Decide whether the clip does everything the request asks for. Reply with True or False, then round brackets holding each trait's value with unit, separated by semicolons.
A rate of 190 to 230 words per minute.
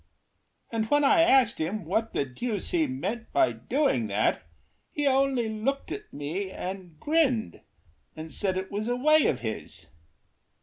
False (160 wpm)